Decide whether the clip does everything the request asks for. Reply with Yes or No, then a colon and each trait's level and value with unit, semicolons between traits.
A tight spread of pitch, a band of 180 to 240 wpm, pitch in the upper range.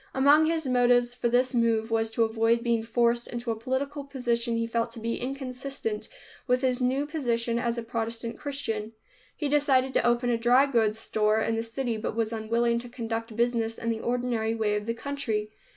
Yes: narrow, 1.9 semitones; average, 200 wpm; high, 235 Hz